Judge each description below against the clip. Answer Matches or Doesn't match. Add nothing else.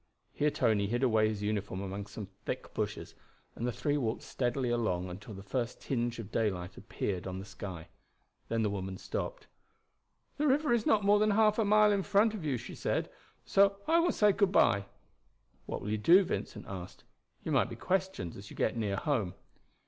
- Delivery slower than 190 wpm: Doesn't match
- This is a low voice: Matches